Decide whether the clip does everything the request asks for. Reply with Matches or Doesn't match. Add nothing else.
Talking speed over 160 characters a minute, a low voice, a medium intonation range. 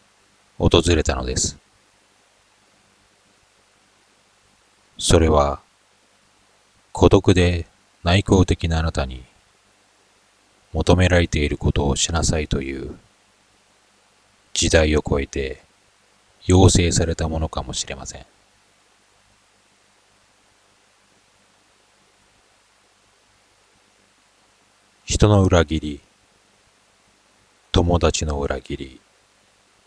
Doesn't match